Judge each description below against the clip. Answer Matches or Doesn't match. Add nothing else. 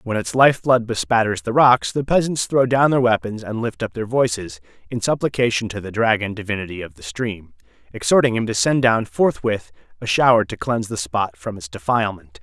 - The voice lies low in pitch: Matches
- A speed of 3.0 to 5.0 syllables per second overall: Doesn't match